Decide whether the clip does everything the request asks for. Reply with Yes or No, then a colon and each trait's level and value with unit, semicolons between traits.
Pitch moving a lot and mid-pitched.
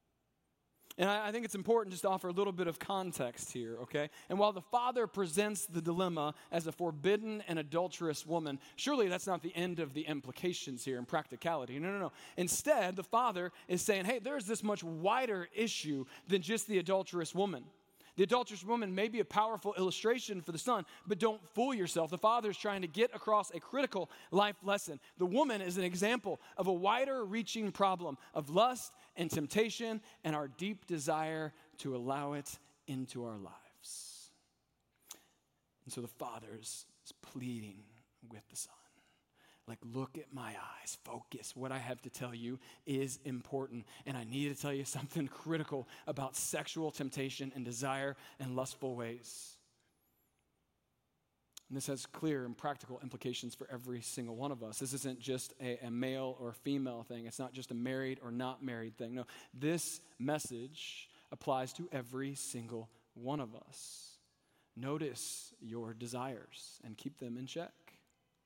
Yes: wide, 6.8 semitones; medium, 150 Hz